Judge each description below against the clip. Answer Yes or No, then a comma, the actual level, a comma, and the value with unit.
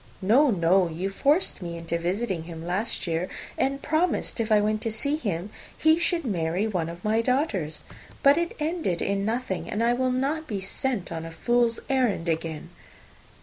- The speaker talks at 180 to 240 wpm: Yes, average, 185 wpm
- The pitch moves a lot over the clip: Yes, wide, 7.3 semitones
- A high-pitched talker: Yes, high, 215 Hz